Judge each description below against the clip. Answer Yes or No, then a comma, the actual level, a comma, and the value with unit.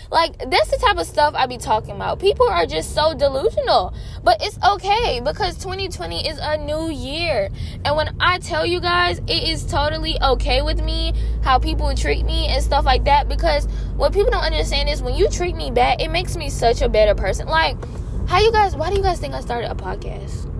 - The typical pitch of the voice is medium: No, very high, 345 Hz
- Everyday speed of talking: No, fast, 220 wpm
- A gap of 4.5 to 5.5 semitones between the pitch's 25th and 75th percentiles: Yes, average, 5.2 semitones